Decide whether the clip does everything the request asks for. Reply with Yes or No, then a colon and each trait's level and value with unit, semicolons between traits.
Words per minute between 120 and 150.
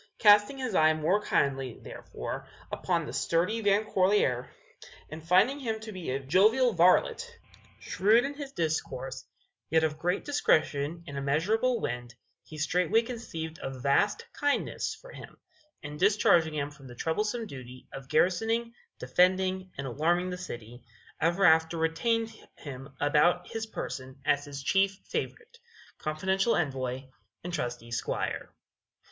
Yes: average, 140 wpm